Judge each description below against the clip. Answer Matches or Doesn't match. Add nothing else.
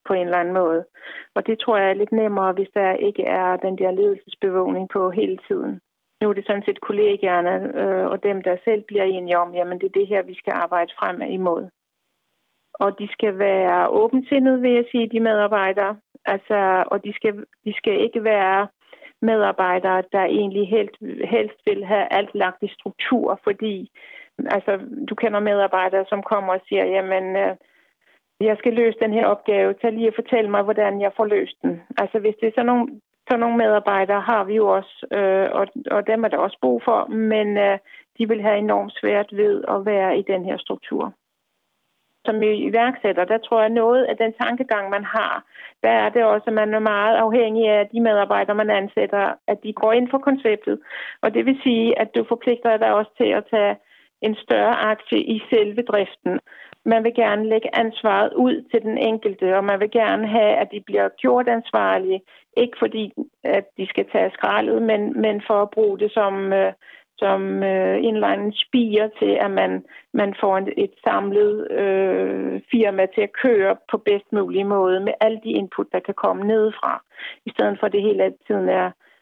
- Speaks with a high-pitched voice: Matches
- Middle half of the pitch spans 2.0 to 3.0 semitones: Matches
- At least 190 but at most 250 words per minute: Matches